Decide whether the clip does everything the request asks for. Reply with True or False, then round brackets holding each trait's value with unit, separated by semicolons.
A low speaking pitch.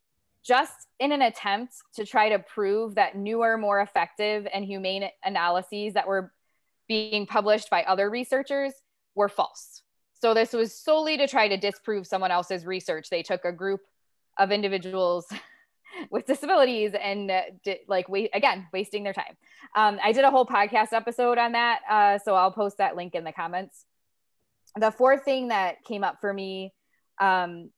False (205 Hz)